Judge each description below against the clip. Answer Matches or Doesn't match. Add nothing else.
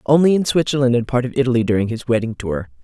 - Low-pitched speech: Matches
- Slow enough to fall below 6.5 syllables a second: Doesn't match